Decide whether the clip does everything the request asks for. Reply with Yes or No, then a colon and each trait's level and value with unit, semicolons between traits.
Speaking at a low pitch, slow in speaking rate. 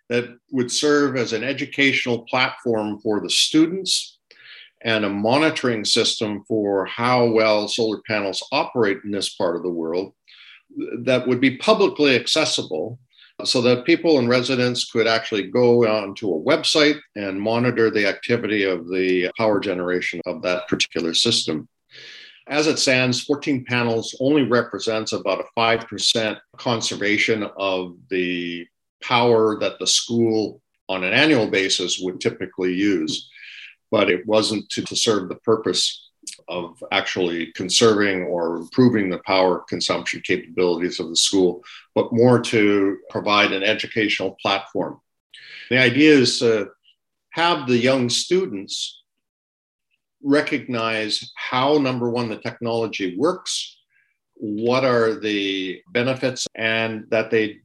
Yes: low, 115 Hz; slow, 130 wpm